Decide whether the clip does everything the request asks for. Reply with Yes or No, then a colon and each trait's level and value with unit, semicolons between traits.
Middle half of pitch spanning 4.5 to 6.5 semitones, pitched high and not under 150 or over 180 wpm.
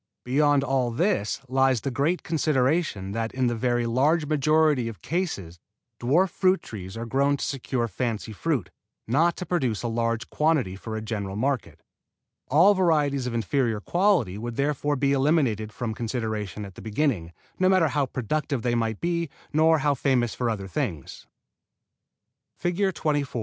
No: average, 5.2 semitones; low, 130 Hz; average, 160 wpm